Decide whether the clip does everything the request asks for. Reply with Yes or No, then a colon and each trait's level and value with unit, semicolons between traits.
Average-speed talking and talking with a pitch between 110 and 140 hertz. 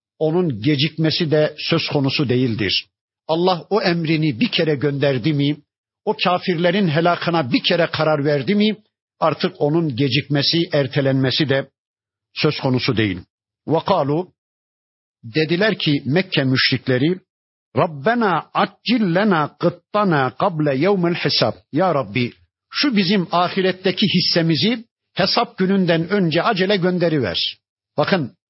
No: average, 110 wpm; medium, 155 Hz